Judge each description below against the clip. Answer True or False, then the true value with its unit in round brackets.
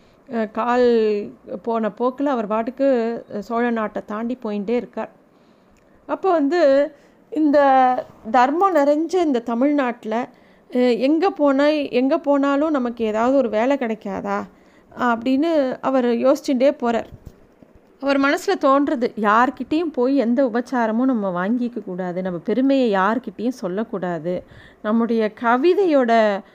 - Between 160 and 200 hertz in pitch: False (245 Hz)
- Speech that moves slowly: False (105 wpm)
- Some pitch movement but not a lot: True (4.2 semitones)